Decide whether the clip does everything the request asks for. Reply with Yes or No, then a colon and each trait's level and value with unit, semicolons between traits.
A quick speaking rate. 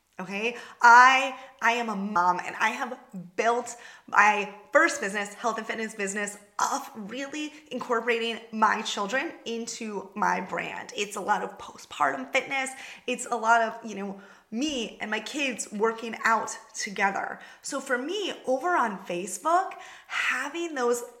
No: average, 145 wpm